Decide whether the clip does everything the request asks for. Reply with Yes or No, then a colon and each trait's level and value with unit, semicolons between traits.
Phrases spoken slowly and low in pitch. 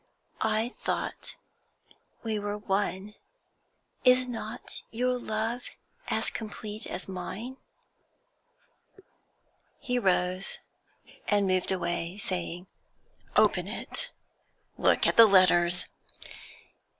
No: slow, 90 wpm; high, 205 Hz